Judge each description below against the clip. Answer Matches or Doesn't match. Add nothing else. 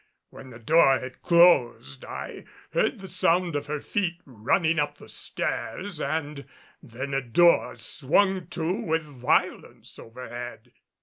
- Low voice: Doesn't match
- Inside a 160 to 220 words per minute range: Doesn't match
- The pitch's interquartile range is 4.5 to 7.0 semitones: Matches